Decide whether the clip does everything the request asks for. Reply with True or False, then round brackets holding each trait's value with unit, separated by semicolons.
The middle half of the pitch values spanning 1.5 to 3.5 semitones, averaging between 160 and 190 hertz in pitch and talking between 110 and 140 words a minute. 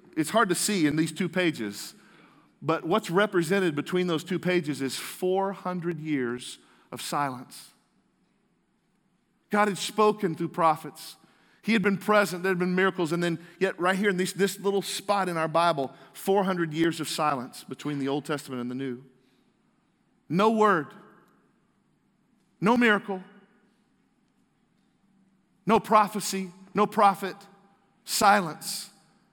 False (4.1 semitones; 185 Hz; 135 wpm)